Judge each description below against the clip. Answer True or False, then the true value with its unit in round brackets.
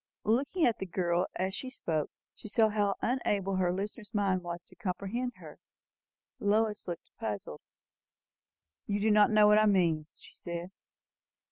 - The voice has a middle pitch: False (200 Hz)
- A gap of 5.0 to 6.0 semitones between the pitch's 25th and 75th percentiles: False (3.3 semitones)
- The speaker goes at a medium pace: True (155 wpm)